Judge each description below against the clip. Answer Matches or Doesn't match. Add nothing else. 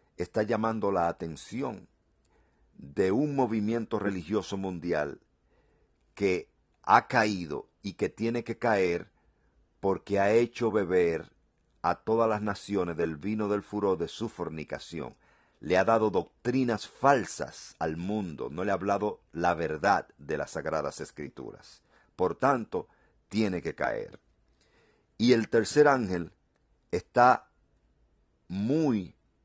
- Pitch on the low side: Matches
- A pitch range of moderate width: Matches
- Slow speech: Matches